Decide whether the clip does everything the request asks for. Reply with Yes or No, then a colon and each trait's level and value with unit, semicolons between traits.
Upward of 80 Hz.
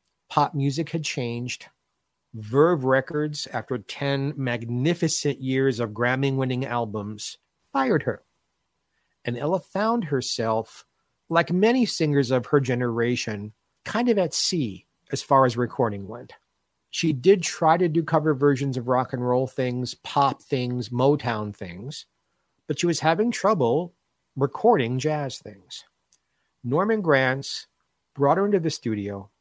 Yes: low, 135 Hz